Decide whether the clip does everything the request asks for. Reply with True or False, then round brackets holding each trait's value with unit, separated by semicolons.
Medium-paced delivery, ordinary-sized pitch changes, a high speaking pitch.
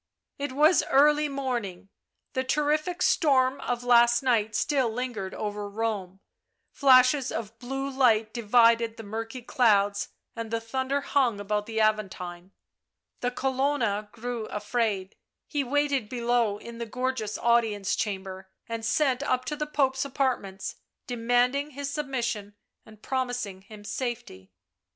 False (130 wpm; 3.9 semitones; 235 Hz)